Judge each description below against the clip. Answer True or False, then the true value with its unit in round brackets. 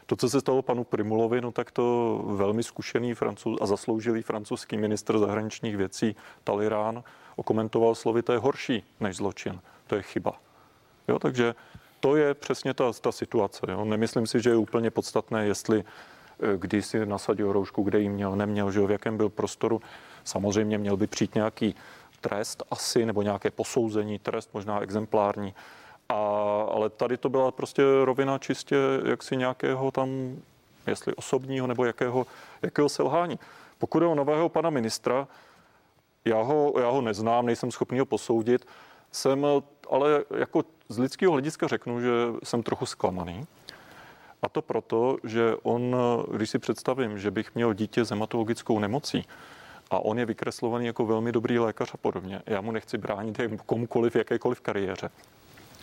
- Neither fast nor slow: True (160 wpm)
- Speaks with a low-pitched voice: True (115 Hz)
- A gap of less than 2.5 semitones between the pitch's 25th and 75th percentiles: False (2.9 semitones)